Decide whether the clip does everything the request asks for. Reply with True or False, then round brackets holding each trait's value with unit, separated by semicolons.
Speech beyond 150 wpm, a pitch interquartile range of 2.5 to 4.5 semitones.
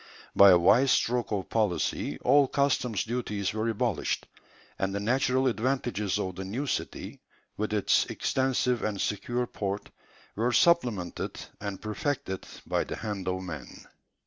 False (145 wpm; 4.2 semitones)